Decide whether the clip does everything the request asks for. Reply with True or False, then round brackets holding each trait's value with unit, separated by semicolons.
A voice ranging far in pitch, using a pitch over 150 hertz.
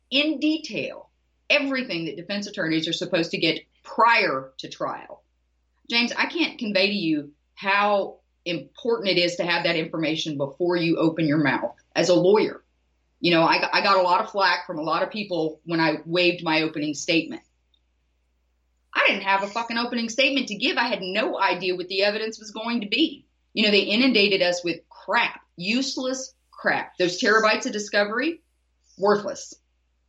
True (6.2 semitones; 185 Hz)